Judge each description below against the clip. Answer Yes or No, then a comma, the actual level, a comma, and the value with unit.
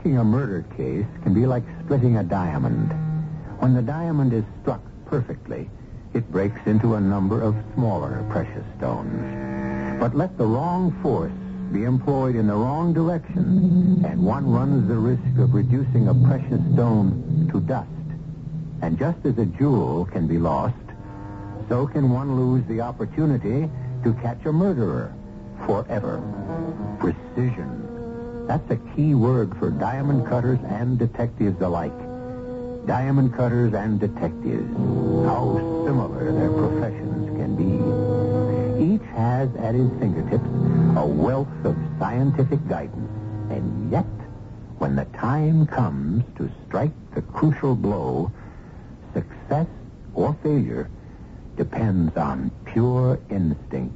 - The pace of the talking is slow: Yes, slow, 130 wpm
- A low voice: Yes, low, 125 Hz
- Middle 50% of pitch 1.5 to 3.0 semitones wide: No, average, 5.0 semitones